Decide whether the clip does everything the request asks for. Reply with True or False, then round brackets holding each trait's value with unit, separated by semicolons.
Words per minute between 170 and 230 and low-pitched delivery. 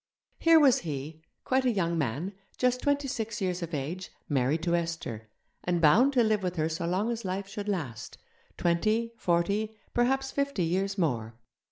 False (175 wpm; 185 Hz)